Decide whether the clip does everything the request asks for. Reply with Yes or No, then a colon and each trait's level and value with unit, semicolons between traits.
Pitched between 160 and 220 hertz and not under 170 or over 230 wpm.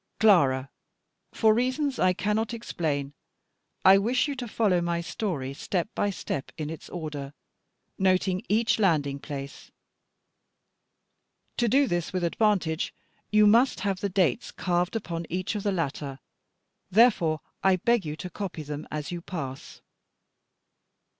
No: medium, 185 Hz; average, 140 wpm